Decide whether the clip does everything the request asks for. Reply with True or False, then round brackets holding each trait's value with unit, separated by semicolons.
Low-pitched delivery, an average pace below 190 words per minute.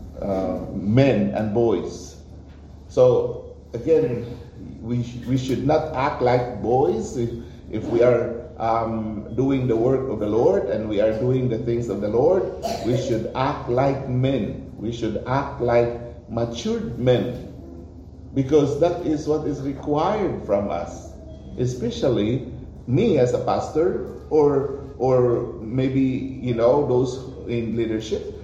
True (120 Hz; 140 wpm)